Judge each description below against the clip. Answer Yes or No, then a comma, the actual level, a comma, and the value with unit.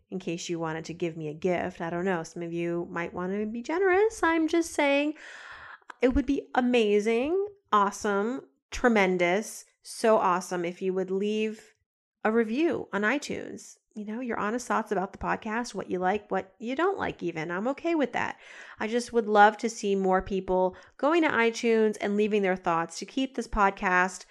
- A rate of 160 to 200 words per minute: Yes, average, 195 wpm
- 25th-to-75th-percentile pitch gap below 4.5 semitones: No, average, 5.2 semitones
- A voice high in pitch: Yes, high, 210 Hz